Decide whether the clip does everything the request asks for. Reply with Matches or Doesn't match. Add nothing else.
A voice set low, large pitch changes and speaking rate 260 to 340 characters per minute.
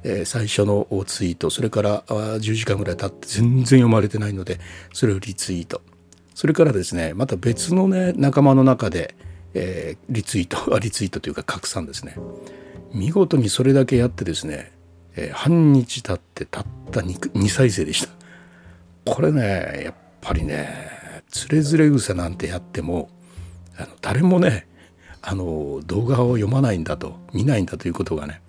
Matches